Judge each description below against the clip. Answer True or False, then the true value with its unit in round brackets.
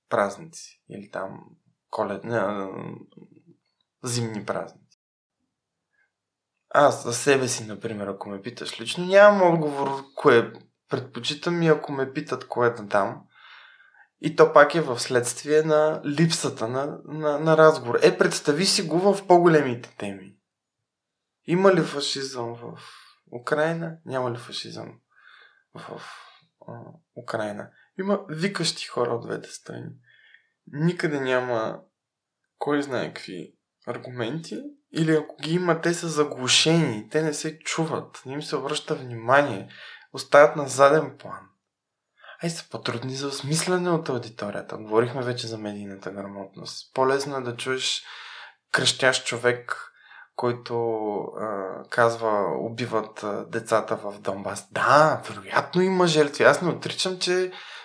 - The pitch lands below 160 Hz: True (140 Hz)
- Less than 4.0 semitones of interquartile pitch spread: False (5.1 semitones)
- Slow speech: False (130 wpm)